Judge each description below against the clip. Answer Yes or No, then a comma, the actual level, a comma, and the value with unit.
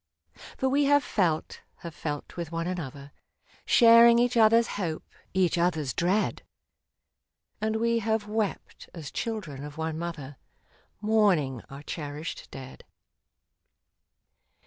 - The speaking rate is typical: No, slow, 125 wpm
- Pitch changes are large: Yes, wide, 6.7 semitones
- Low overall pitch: No, medium, 175 Hz